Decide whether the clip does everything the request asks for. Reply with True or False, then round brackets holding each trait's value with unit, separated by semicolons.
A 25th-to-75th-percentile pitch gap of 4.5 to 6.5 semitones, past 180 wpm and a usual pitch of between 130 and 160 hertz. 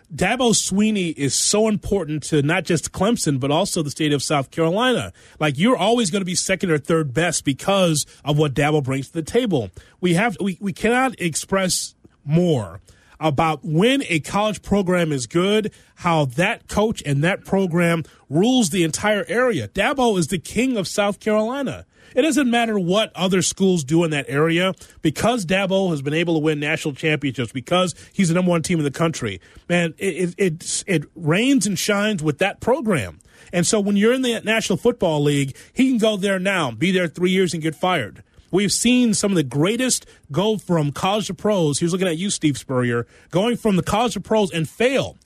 False (5.0 semitones; 200 wpm; 180 Hz)